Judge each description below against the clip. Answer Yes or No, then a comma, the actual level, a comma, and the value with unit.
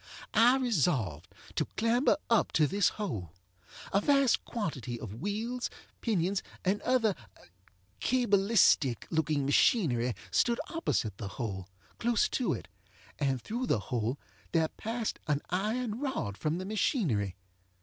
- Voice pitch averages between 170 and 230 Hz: Yes, high, 190 Hz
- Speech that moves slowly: Yes, slow, 130 wpm